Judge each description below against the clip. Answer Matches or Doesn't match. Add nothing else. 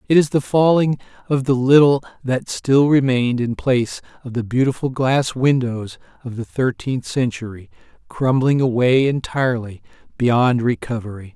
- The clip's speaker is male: Matches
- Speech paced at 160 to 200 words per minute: Doesn't match